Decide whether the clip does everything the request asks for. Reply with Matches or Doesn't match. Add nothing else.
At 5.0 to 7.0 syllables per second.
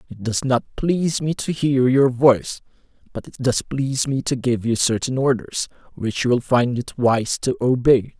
Doesn't match